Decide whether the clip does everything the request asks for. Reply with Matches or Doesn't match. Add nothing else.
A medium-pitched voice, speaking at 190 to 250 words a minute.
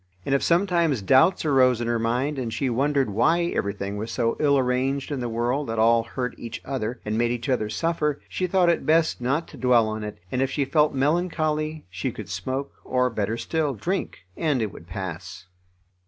Doesn't match